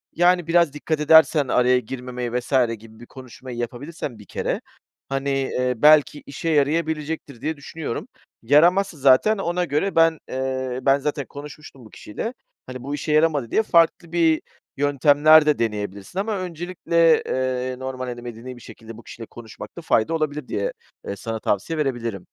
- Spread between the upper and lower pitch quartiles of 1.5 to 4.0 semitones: No, average, 4.4 semitones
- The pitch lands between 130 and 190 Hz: Yes, medium, 140 Hz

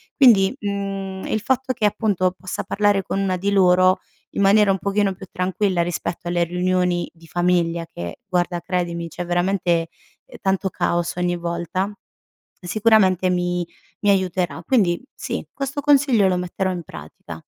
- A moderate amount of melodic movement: No, narrow, 2.2 semitones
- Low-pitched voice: No, medium, 185 Hz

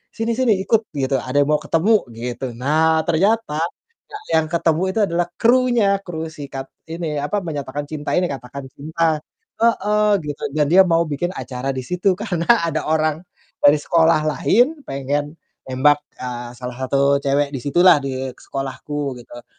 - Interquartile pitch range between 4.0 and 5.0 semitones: Yes, average, 4.5 semitones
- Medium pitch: Yes, medium, 155 Hz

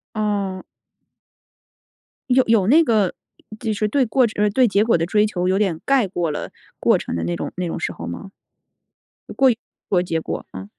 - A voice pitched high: Yes, high, 205 Hz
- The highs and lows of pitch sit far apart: No, average, 4.3 semitones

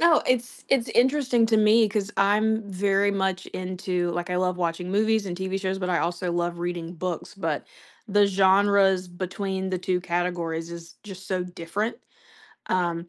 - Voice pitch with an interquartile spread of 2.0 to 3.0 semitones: Yes, narrow, 2.5 semitones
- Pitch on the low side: No, medium, 185 Hz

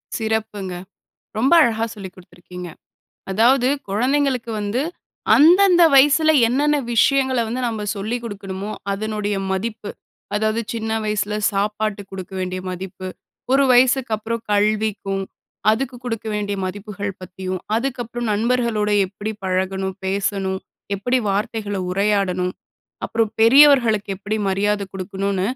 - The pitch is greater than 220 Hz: No, high, 210 Hz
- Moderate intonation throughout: Yes, average, 3.3 semitones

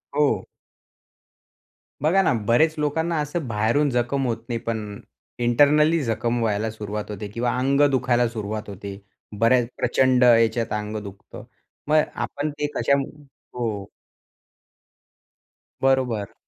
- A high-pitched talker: No, low, 120 Hz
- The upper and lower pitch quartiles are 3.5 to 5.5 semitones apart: Yes, average, 4.3 semitones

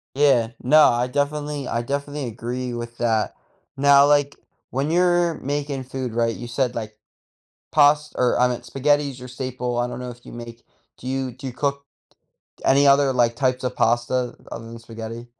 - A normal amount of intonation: Yes, average, 3.0 semitones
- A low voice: Yes, low, 130 Hz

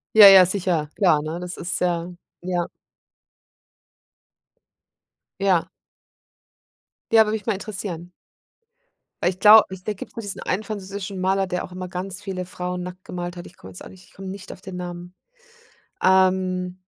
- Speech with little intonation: Yes, narrow, 1.6 semitones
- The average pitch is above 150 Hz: Yes, medium, 185 Hz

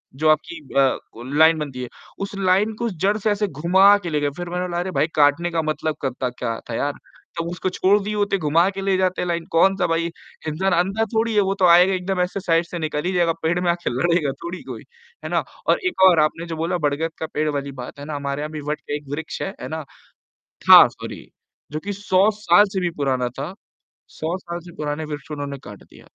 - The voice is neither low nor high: Yes, medium, 170 Hz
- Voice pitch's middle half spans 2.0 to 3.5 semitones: No, average, 4.0 semitones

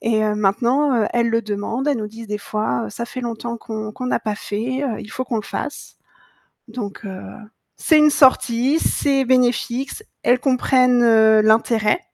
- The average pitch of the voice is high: Yes, high, 235 Hz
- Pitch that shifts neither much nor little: Yes, average, 3.1 semitones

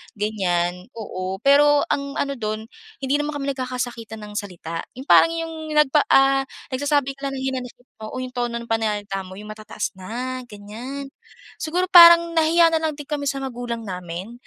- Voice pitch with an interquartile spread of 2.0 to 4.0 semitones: No, average, 5.1 semitones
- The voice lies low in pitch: No, very high, 255 Hz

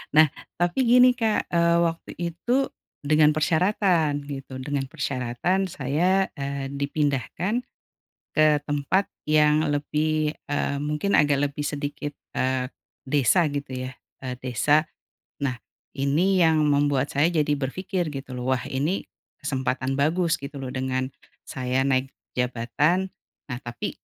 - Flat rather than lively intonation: No, average, 3.5 semitones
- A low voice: No, medium, 145 Hz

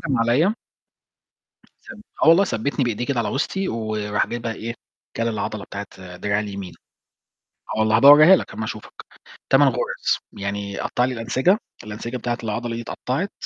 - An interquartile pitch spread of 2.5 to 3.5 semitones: No, average, 4.1 semitones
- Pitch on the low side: Yes, low, 115 Hz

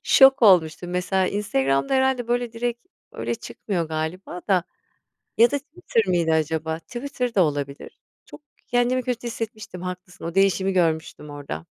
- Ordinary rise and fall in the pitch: No, wide, 6.9 semitones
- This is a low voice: No, high, 190 Hz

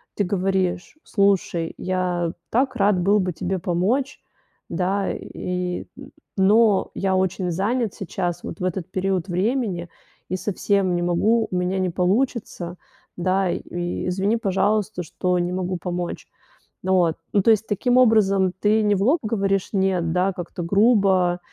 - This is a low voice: No, high, 190 Hz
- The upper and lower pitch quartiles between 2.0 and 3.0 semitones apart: Yes, narrow, 2.4 semitones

